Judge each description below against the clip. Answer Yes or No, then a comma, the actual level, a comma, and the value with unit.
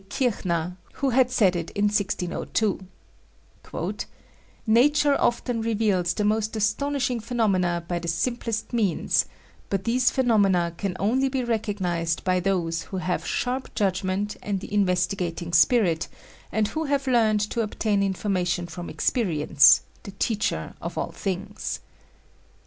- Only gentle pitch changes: No, average, 4.5 semitones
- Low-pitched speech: No, high, 205 Hz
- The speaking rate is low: Yes, slow, 130 wpm